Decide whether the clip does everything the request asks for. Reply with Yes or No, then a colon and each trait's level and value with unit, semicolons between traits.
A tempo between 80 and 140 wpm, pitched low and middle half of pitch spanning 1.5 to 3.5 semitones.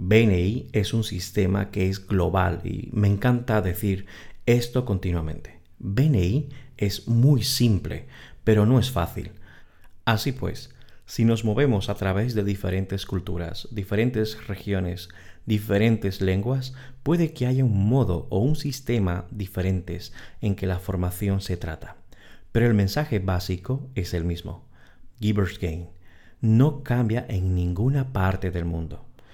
No: average, 135 wpm; low, 100 Hz; average, 4.5 semitones